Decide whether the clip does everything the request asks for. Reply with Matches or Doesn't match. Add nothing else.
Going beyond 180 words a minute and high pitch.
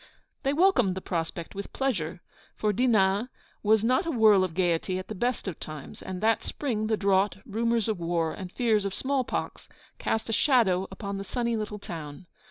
Matches